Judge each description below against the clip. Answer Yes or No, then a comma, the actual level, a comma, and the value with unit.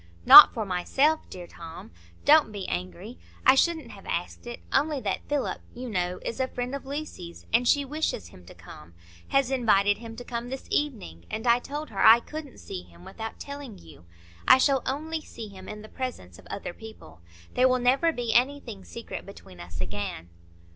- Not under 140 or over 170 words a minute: No, average, 195 wpm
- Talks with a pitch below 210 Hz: No, high, 235 Hz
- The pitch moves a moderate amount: No, wide, 7.2 semitones